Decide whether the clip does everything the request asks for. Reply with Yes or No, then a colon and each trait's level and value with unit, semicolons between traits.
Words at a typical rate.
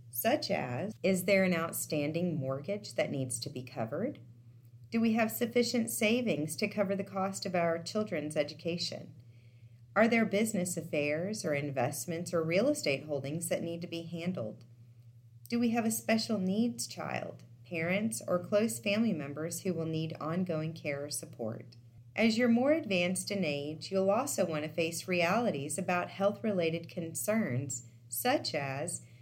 Yes: average, 160 wpm